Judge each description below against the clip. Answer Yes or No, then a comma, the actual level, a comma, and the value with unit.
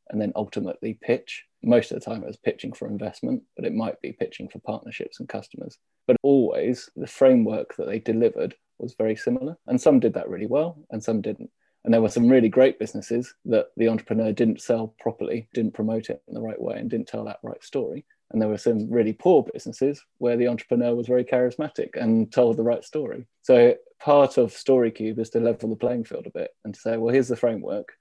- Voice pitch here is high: No, low, 120 Hz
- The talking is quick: Yes, fast, 225 wpm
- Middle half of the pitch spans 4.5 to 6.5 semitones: No, average, 3.8 semitones